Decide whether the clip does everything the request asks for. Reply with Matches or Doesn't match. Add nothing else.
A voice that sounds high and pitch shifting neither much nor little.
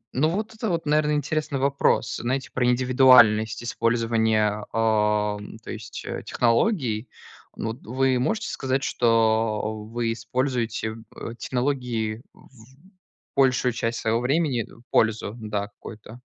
Doesn't match